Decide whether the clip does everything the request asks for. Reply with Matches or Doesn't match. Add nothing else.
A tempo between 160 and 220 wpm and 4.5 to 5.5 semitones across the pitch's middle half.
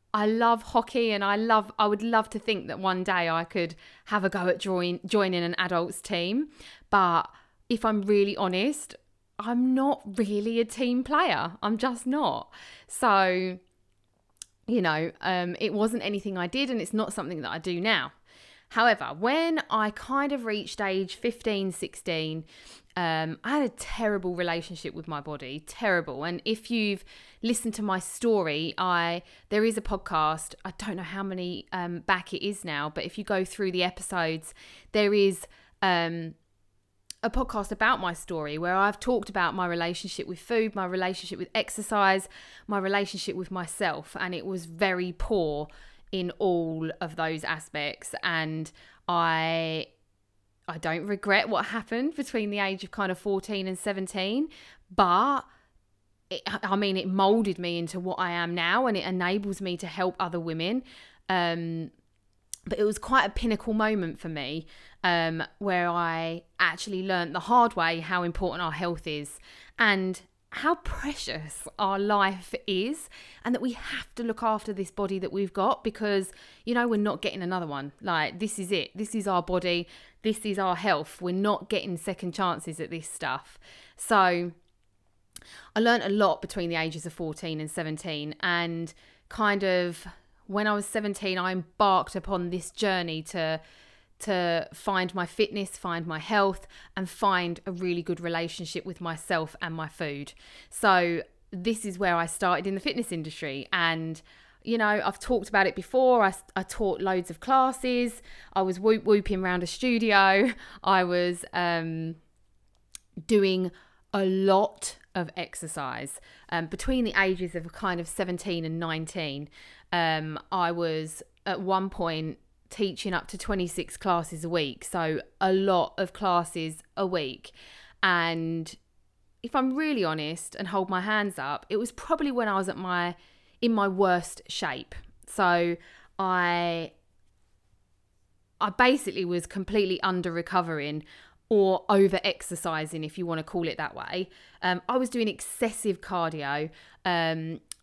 Doesn't match